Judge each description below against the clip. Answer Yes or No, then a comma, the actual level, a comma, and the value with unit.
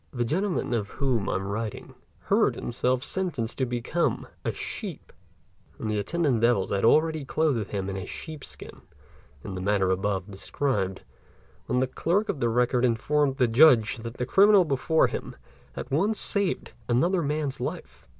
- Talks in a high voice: No, low, 125 Hz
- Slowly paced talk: No, average, 170 wpm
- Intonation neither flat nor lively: No, wide, 6.3 semitones